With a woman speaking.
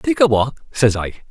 No: male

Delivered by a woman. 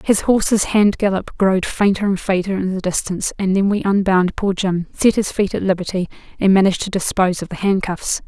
Yes: female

